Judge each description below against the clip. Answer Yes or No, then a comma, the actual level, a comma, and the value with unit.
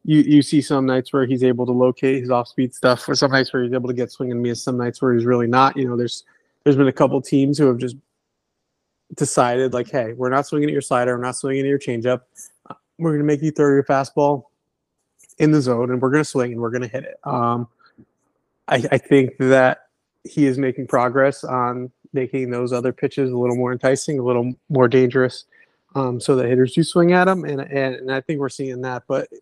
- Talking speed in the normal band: No, fast, 240 wpm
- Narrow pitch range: Yes, narrow, 2.0 semitones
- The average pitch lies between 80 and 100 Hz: No, low, 130 Hz